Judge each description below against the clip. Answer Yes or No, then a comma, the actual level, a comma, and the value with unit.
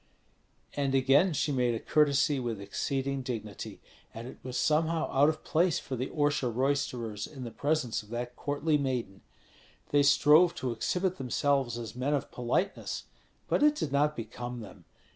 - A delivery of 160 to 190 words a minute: Yes, average, 165 wpm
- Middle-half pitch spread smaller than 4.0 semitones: Yes, average, 3.5 semitones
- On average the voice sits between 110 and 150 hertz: Yes, low, 135 Hz